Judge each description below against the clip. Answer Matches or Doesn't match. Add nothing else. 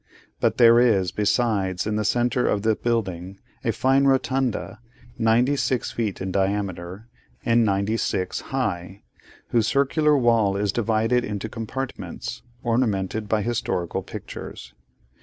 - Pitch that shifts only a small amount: Doesn't match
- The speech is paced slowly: Matches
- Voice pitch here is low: Matches